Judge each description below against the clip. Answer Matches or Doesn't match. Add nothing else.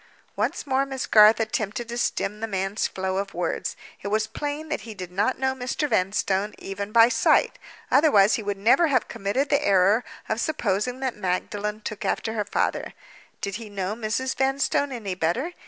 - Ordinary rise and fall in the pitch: Matches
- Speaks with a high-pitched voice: Matches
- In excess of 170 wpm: Matches